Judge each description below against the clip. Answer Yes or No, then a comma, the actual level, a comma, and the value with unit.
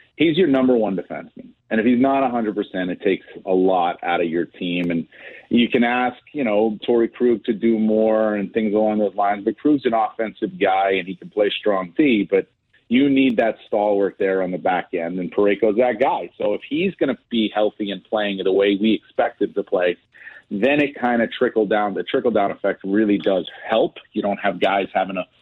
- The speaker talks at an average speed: No, fast, 220 wpm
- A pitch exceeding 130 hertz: No, low, 105 Hz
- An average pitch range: Yes, average, 3.3 semitones